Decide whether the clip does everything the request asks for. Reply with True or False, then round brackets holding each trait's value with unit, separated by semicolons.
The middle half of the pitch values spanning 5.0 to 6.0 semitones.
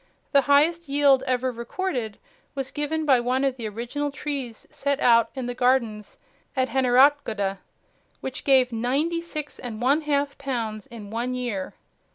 False (3.3 semitones)